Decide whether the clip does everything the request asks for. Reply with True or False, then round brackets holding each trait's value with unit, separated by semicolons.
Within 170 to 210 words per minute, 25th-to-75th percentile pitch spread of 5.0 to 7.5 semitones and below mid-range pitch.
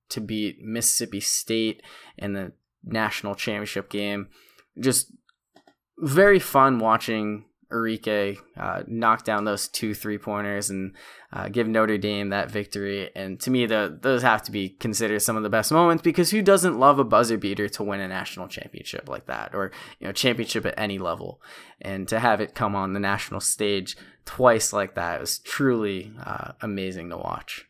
False (175 wpm; 2.5 semitones; 105 Hz)